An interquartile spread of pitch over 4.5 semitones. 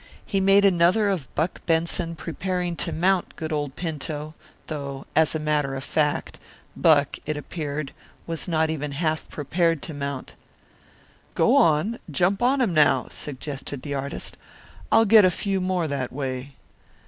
No: average, 3.9 semitones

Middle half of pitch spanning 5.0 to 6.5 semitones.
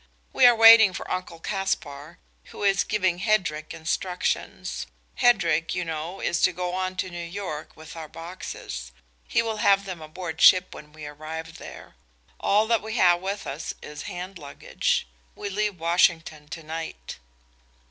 No: average, 3.7 semitones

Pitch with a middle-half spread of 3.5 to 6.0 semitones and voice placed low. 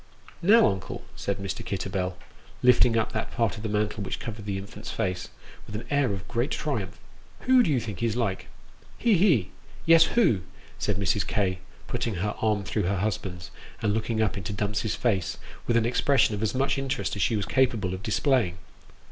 Yes: average, 3.9 semitones; low, 105 Hz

